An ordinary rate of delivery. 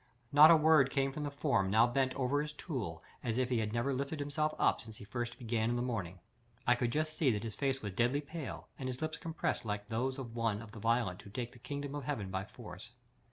No: fast, 250 wpm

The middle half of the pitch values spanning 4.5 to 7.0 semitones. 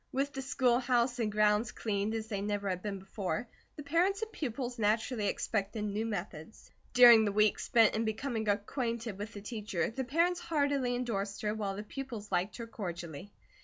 No: average, 3.4 semitones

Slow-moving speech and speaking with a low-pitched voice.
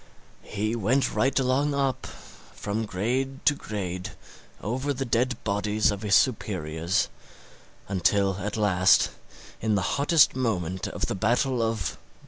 Yes: slow, 130 wpm; low, 110 Hz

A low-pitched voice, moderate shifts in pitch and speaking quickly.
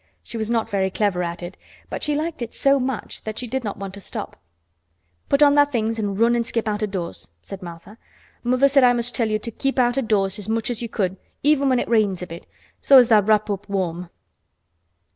No: high, 220 Hz; average, 3.9 semitones; fast, 240 wpm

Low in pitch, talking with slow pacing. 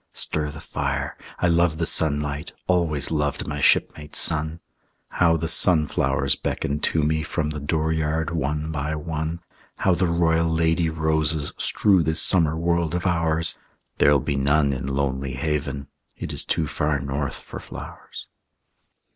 No: very low, 80 Hz; average, 150 wpm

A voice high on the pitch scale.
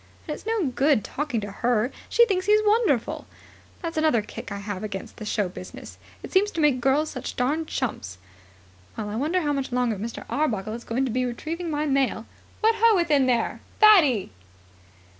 Yes: very high, 270 Hz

